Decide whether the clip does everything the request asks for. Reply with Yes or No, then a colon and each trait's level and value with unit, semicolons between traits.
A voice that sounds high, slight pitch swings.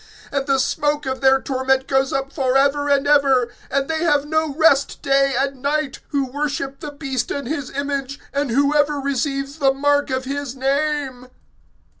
Yes: very high, 275 Hz; narrow, 1.3 semitones